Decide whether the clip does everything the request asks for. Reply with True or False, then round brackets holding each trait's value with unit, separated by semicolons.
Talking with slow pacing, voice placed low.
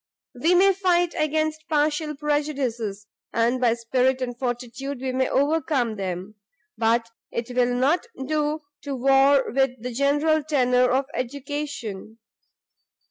False (130 wpm; 265 Hz)